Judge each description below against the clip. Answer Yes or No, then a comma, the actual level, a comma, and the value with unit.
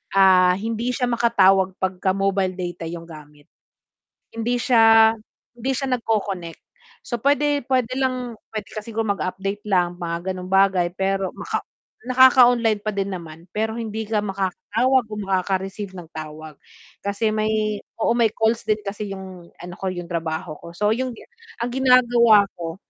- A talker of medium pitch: No, high, 200 Hz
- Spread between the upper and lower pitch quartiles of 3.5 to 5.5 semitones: Yes, average, 3.8 semitones